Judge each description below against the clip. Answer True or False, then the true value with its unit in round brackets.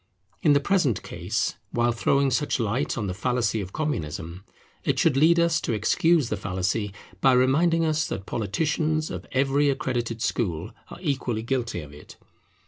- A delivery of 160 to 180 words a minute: True (165 wpm)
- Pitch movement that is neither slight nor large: False (6.2 semitones)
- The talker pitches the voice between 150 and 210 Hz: False (125 Hz)